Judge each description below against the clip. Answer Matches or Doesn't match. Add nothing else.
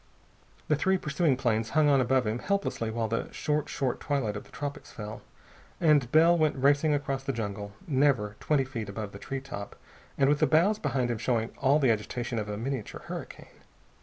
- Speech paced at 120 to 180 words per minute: Doesn't match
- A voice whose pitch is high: Doesn't match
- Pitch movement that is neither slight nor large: Matches